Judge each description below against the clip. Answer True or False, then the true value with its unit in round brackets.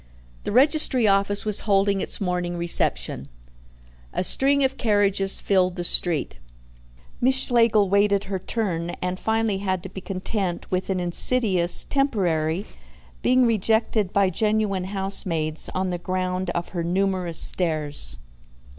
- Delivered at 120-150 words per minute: True (135 wpm)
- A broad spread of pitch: False (3.2 semitones)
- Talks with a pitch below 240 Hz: True (190 Hz)